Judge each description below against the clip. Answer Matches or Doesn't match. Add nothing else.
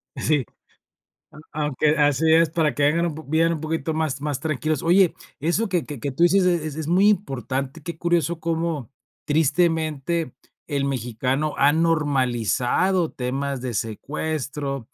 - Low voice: Doesn't match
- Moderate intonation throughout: Matches